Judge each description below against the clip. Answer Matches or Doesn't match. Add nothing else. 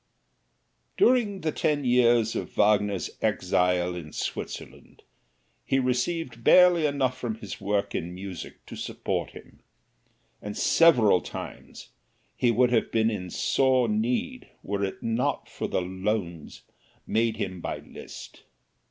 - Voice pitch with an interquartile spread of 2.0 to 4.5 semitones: Doesn't match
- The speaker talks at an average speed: Doesn't match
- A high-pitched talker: Doesn't match